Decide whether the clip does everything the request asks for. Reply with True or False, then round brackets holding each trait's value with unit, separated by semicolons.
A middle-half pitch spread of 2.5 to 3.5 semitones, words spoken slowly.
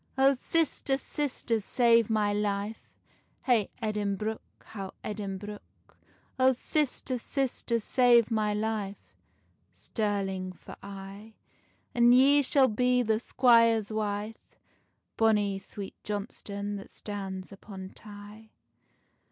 True (2.9 semitones; 100 wpm)